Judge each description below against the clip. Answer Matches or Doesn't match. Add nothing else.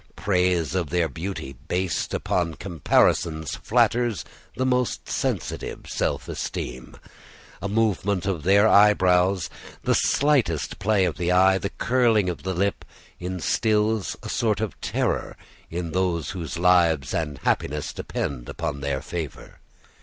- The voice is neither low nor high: Doesn't match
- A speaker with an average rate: Doesn't match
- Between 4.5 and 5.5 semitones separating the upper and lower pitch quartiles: Doesn't match